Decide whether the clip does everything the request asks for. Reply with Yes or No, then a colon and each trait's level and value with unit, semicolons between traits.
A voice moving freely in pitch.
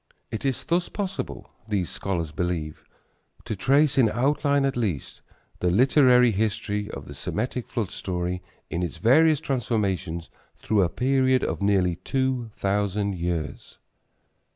Yes: wide, 6.2 semitones